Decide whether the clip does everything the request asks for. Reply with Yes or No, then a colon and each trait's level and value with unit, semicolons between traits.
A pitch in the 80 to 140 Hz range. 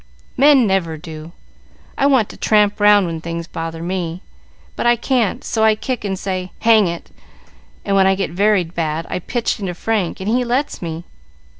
No: high, 195 Hz